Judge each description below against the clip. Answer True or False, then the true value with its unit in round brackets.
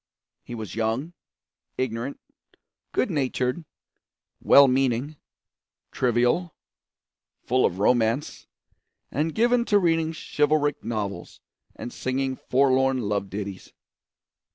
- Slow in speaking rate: True (95 wpm)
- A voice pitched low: True (130 Hz)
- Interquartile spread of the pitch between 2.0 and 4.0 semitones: False (4.5 semitones)